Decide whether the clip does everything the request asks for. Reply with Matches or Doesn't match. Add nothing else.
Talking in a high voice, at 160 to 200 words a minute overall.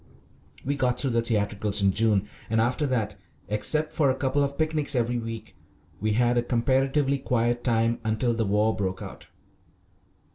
Doesn't match